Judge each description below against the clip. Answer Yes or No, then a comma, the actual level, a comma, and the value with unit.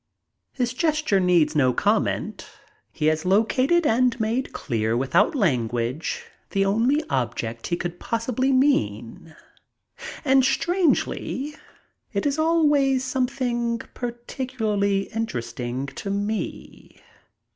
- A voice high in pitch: Yes, high, 225 Hz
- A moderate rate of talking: No, slow, 105 wpm